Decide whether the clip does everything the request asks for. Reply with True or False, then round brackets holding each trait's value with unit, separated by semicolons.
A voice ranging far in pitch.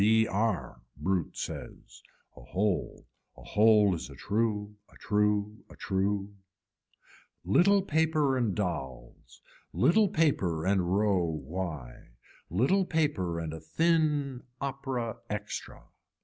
True (6.9 semitones)